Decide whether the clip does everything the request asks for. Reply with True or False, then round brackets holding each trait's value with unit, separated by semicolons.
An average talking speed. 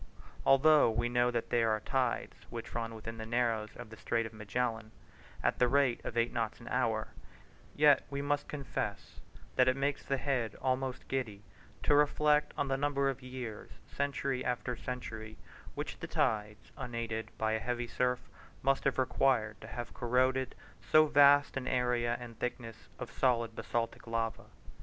True (170 wpm)